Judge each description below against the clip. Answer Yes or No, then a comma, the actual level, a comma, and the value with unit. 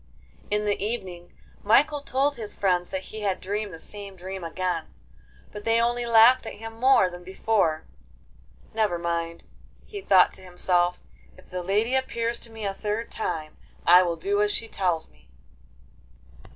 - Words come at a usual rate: Yes, average, 165 wpm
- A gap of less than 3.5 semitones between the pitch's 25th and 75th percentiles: No, average, 4.1 semitones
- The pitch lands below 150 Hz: No, high, 200 Hz